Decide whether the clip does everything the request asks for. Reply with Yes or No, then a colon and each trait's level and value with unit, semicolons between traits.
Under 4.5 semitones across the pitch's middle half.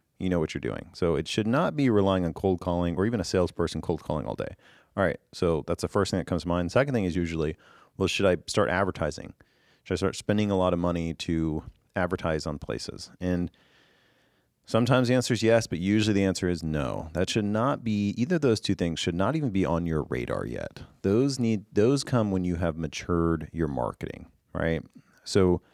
Yes: average, 4.1 semitones